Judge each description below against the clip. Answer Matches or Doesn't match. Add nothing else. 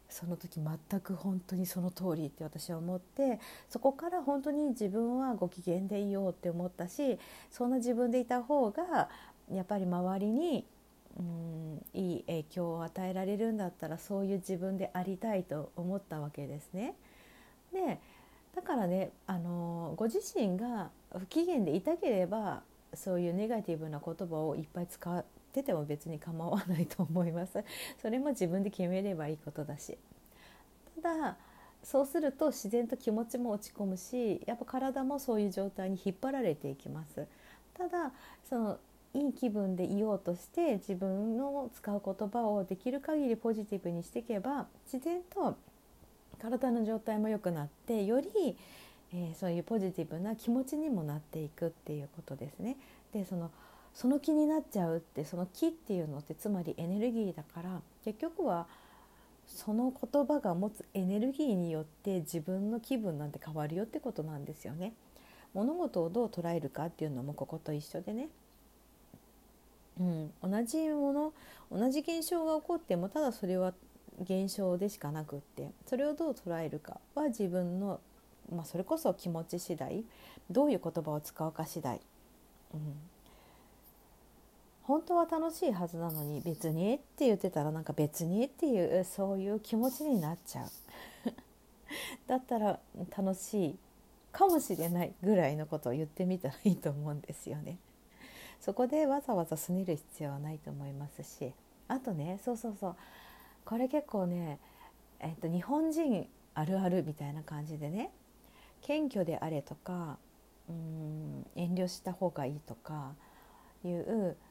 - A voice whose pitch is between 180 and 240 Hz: Matches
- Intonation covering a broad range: Matches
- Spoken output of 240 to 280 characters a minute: Doesn't match